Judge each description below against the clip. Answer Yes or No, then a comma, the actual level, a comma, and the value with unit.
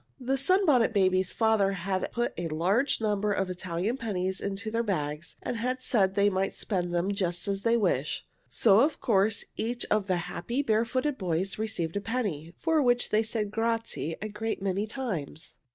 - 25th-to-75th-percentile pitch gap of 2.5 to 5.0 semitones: Yes, average, 3.7 semitones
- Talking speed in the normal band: Yes, average, 180 wpm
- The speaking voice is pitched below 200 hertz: No, high, 205 Hz